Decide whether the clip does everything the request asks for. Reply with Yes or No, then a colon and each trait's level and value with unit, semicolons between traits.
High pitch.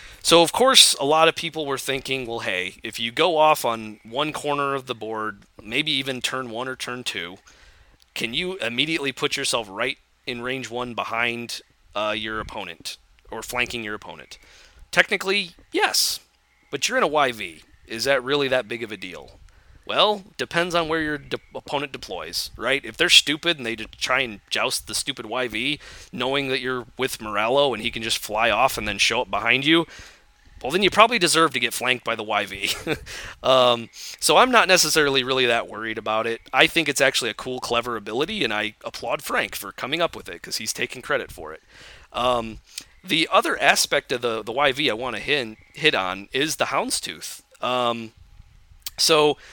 No: low, 125 Hz